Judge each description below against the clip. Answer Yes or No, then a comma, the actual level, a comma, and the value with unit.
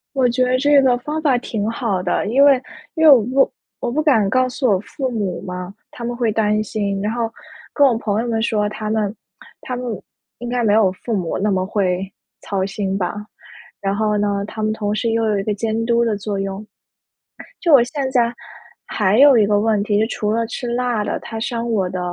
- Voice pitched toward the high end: Yes, high, 220 Hz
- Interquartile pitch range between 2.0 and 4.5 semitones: Yes, average, 3.1 semitones